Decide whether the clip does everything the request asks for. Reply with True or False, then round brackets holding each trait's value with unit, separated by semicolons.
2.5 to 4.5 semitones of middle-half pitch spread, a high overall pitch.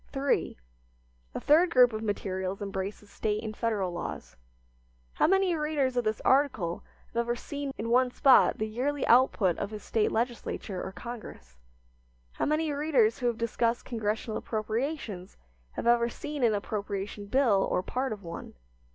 True (4.2 semitones; 230 Hz)